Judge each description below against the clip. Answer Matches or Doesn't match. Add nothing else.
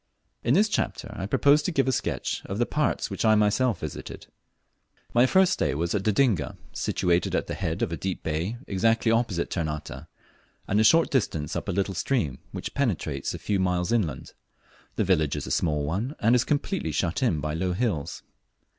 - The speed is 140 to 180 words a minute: Doesn't match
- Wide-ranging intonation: Matches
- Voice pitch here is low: Matches